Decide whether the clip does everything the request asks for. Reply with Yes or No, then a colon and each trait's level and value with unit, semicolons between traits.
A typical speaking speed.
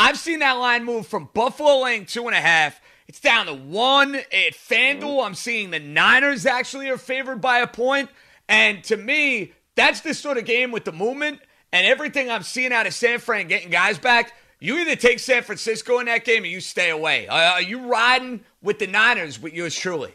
No: fast, 215 wpm